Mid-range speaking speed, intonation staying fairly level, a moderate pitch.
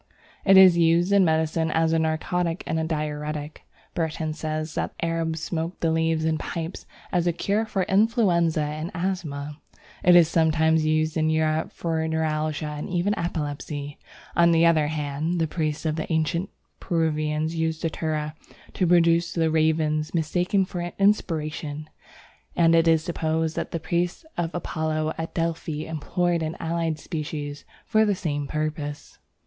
Yes: average, 155 wpm; narrow, 1.7 semitones; medium, 160 Hz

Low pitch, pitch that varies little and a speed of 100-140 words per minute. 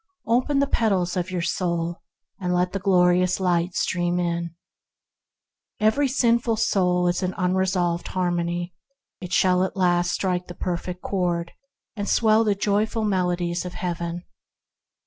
No: medium, 180 Hz; narrow, 2.2 semitones; slow, 135 wpm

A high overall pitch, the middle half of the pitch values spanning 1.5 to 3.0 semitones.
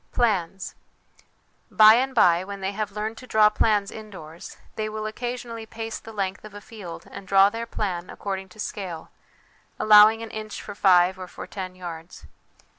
Yes: high, 210 Hz; narrow, 2.5 semitones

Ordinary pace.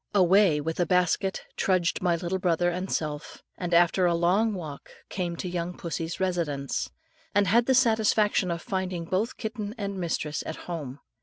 Yes: average, 170 wpm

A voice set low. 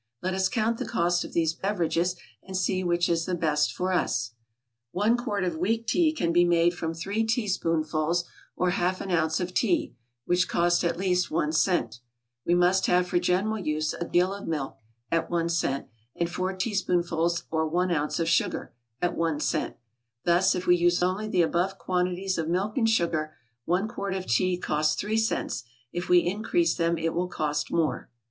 No: medium, 175 Hz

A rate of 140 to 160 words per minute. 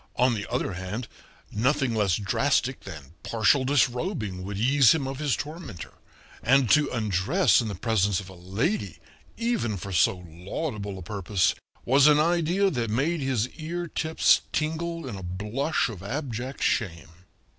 Yes: average, 155 wpm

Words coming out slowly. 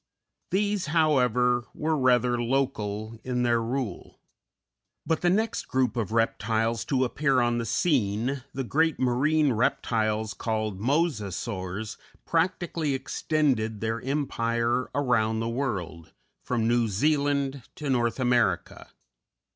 Yes: slow, 115 wpm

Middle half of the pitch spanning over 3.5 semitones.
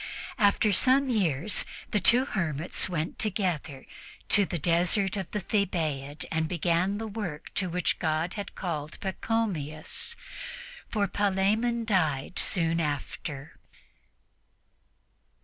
Yes: average, 4.5 semitones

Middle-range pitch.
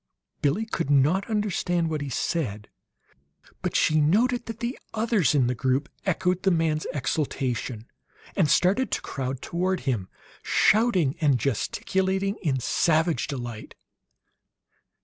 Yes: medium, 160 Hz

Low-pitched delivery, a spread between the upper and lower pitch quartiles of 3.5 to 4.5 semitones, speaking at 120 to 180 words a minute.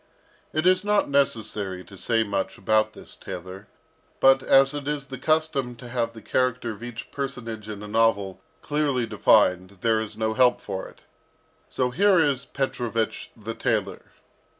Yes: low, 115 Hz; average, 4.1 semitones; average, 165 wpm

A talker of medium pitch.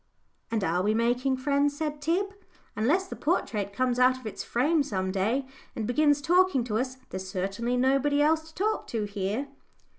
No: very high, 255 Hz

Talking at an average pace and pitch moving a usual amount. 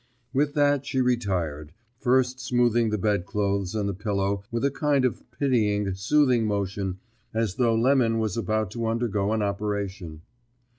Yes: average, 150 wpm; average, 3.8 semitones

